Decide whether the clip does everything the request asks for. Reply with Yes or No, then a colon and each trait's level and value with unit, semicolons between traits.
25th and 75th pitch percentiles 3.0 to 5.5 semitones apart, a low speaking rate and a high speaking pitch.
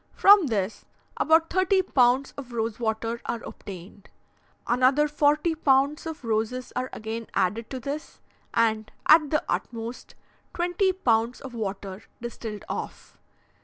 Yes: average, 5.1 semitones; slow, 130 wpm; high, 245 Hz